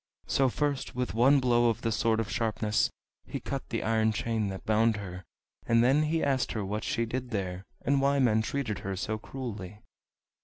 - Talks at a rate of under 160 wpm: No, average, 195 wpm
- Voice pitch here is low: Yes, low, 115 Hz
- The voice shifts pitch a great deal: No, average, 3.3 semitones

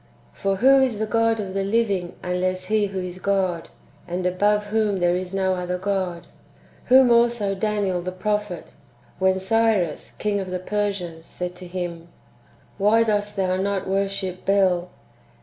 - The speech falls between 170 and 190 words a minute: No, average, 160 wpm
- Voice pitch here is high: Yes, high, 195 Hz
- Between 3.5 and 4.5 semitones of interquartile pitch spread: No, narrow, 2.4 semitones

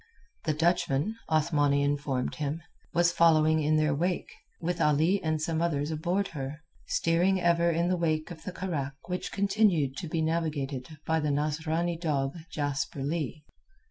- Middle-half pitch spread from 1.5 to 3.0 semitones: Yes, average, 2.7 semitones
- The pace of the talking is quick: No, average, 155 wpm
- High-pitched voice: No, medium, 160 Hz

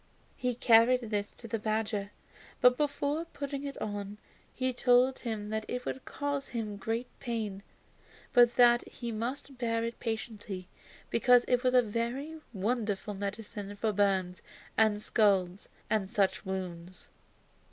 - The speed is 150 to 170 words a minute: No, average, 140 wpm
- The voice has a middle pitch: No, high, 225 Hz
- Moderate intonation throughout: Yes, average, 3.4 semitones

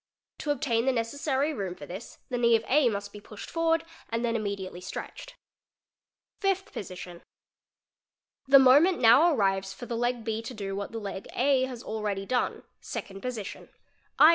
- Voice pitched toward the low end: No, high, 230 Hz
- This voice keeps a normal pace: Yes, average, 165 wpm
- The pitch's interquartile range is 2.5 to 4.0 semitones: No, average, 4.9 semitones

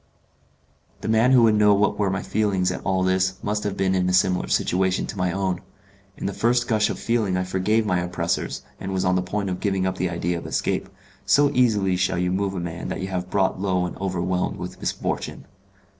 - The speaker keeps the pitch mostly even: Yes, narrow, 2.2 semitones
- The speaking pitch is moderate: No, very low, 95 Hz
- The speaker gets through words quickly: Yes, fast, 225 wpm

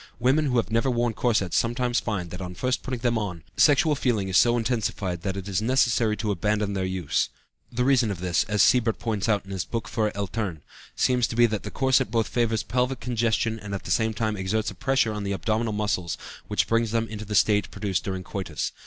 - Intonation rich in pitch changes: No, average, 3.2 semitones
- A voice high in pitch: No, low, 110 Hz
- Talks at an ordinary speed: No, fast, 225 wpm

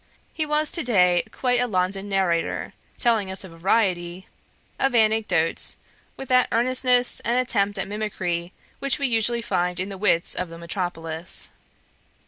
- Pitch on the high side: Yes, high, 200 Hz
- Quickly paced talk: No, average, 150 wpm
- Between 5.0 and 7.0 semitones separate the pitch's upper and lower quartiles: Yes, average, 5.3 semitones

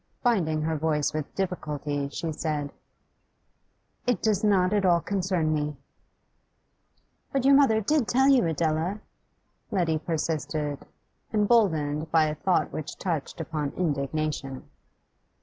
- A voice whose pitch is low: No, medium, 160 Hz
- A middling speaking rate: No, slow, 120 wpm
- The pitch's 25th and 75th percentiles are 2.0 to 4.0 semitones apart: No, average, 4.6 semitones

